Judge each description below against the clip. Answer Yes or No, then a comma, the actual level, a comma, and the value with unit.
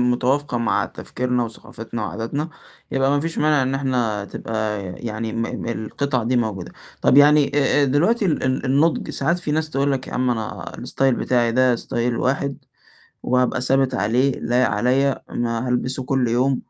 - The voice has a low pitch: Yes, low, 125 Hz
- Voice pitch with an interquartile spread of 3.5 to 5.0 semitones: No, average, 3.0 semitones